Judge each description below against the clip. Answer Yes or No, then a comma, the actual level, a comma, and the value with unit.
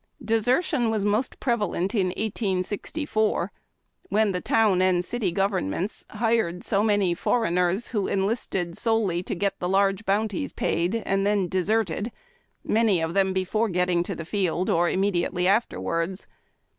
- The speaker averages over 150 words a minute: No, average, 145 wpm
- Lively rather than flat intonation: No, average, 3.4 semitones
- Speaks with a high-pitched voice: Yes, high, 195 Hz